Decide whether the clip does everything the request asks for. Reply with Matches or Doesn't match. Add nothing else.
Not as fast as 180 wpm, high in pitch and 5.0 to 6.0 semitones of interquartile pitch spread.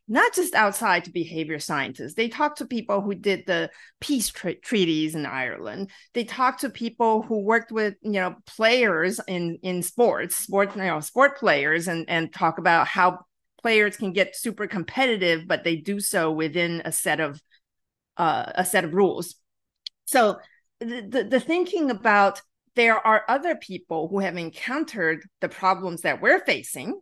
Matches